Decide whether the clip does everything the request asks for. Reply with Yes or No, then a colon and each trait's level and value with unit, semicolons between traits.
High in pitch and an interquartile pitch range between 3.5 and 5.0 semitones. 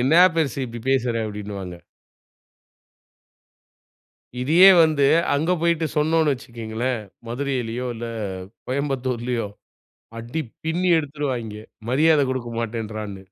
No: low, 125 Hz; average, 4.5 semitones